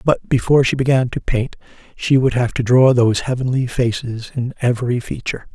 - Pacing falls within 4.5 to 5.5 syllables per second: No, 5.7 syllables/s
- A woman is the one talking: No, male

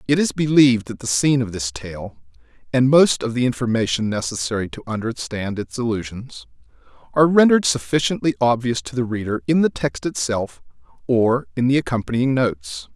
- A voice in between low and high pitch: No, low, 115 Hz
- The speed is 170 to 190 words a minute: No, average, 160 wpm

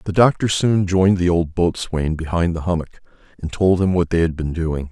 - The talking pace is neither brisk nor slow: No, fast, 220 wpm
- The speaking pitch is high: No, very low, 85 Hz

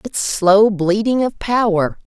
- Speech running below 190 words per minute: Yes, average, 140 wpm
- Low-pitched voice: No, high, 205 Hz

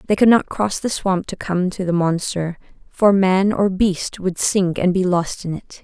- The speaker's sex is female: Yes, female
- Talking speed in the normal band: No, fast, 225 wpm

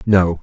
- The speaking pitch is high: No, very low, 90 Hz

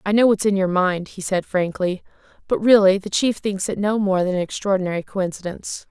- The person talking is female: Yes, female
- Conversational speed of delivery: No, fast, 215 wpm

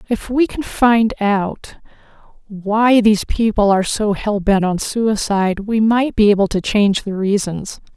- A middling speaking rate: Yes, average, 165 wpm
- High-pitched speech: Yes, high, 210 Hz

